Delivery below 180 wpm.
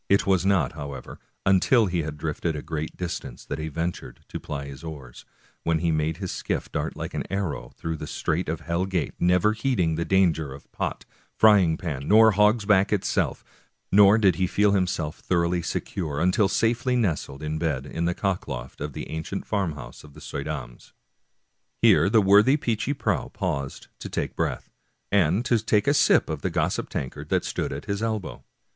No: average, 190 wpm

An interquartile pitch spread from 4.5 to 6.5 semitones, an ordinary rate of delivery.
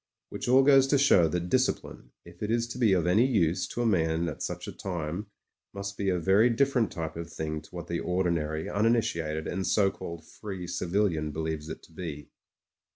No: average, 4.9 semitones; fast, 210 wpm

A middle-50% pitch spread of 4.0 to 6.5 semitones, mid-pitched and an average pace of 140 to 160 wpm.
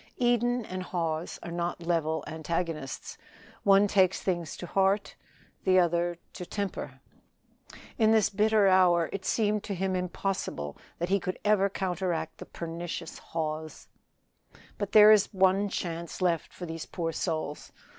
No: average, 2.9 semitones; medium, 180 Hz; average, 145 wpm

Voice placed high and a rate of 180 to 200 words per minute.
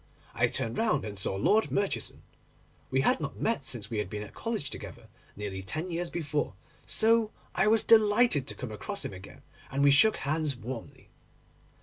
No: medium, 145 Hz; average, 185 wpm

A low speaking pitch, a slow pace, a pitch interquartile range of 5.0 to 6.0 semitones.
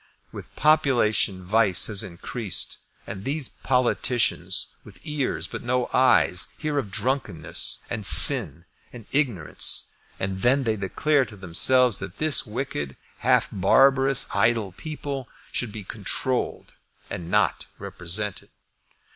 Yes: low, 115 Hz; slow, 120 wpm; wide, 5.5 semitones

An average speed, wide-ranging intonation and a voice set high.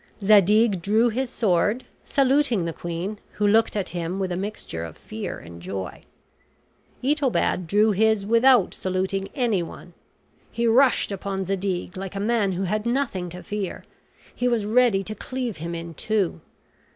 No: average, 155 wpm; average, 4.1 semitones; high, 205 Hz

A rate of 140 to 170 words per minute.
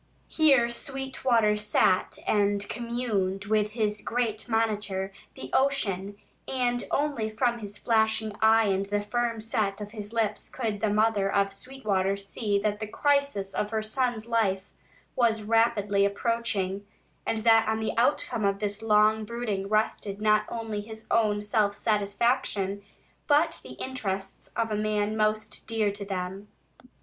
Yes: average, 145 wpm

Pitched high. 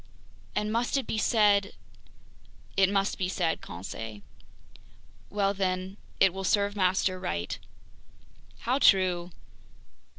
Yes: high, 195 Hz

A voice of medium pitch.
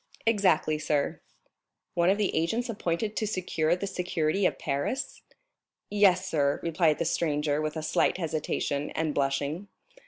Yes: medium, 165 Hz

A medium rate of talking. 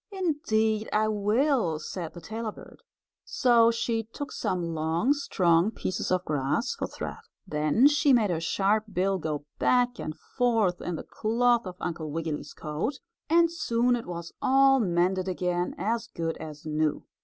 Yes: average, 160 wpm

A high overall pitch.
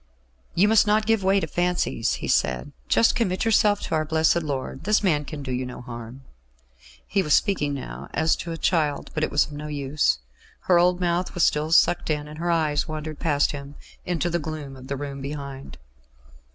No: medium, 155 Hz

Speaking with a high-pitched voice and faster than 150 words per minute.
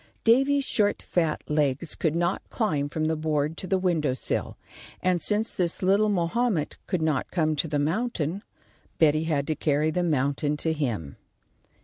No: medium, 160 Hz; average, 165 wpm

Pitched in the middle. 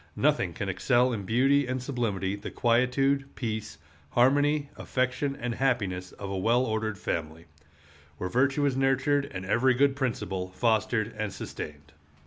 No: low, 120 Hz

